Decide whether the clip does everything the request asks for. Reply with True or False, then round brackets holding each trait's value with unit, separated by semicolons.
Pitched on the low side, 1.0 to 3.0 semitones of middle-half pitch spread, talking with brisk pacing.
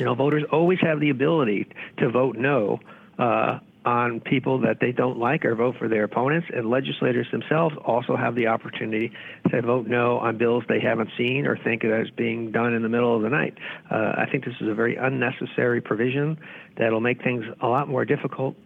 True (120 Hz; 2.6 semitones; 210 wpm)